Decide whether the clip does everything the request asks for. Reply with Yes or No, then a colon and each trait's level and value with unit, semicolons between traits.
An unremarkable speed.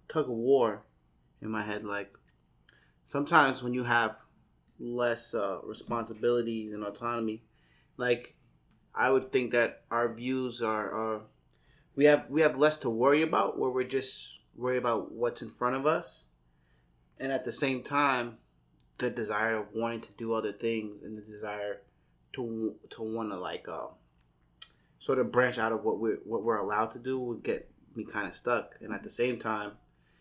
Yes: average, 175 wpm